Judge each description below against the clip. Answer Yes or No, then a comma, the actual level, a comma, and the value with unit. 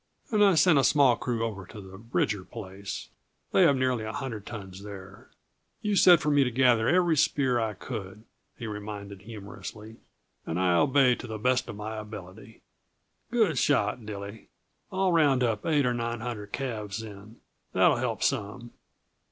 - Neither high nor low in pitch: No, low, 115 Hz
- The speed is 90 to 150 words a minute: No, average, 170 wpm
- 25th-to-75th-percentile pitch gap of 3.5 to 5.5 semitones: Yes, average, 4.4 semitones